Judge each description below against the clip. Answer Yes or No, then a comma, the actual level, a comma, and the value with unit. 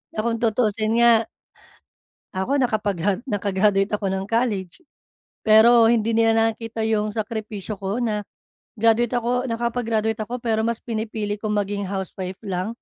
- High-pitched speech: Yes, high, 220 Hz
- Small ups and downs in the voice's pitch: Yes, narrow, 2.0 semitones